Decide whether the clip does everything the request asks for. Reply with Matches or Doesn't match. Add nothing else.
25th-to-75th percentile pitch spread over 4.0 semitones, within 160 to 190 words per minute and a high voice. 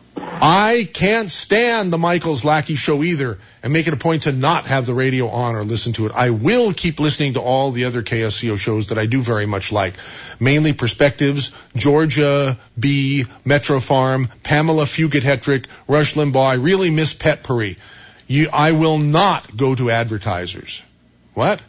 Doesn't match